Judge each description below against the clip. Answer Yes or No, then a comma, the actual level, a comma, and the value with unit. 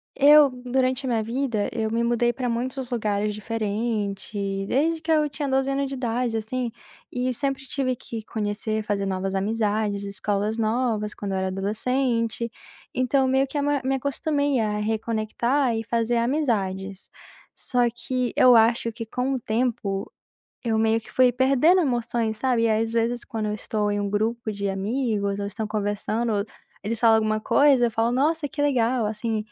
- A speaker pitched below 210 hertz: No, high, 230 Hz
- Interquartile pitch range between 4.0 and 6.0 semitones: No, average, 3.3 semitones